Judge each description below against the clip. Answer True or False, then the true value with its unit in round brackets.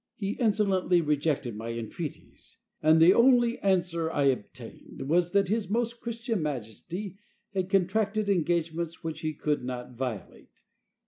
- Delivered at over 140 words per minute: False (135 wpm)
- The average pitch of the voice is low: False (175 Hz)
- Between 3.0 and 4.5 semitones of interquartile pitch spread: False (5.3 semitones)